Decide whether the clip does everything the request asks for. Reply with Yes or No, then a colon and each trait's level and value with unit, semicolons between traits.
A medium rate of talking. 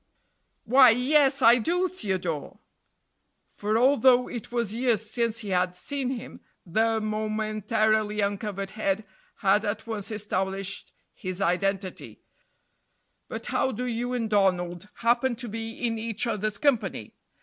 No: slow, 130 wpm